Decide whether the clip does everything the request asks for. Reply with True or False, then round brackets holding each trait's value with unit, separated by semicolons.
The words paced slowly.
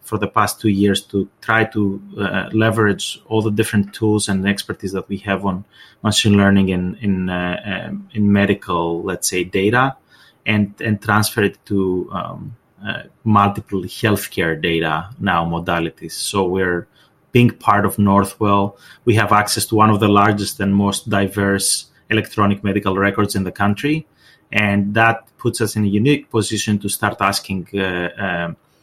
False (165 wpm)